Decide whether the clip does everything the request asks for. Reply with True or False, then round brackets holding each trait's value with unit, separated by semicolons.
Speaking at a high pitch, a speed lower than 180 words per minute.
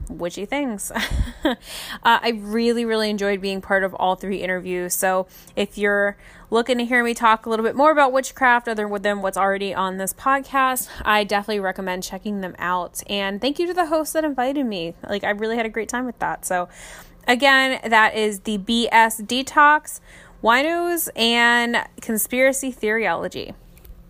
True (220 Hz; 170 wpm)